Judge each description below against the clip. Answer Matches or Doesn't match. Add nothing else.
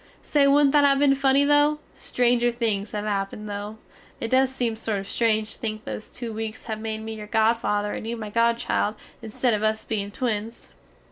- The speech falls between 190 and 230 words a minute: Matches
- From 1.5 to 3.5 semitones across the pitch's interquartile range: Matches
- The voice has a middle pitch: Doesn't match